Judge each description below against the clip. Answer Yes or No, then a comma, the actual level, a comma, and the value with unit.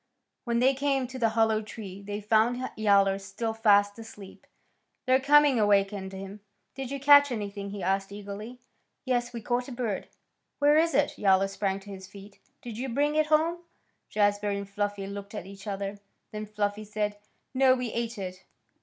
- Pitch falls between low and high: No, high, 215 Hz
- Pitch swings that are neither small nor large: Yes, average, 3.9 semitones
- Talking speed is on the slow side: No, average, 180 wpm